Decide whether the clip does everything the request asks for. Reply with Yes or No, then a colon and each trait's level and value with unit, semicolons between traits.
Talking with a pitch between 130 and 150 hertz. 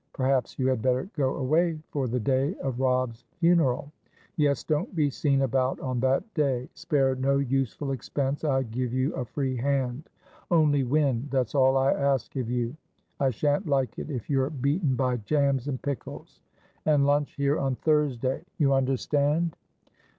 Yes: low, 135 Hz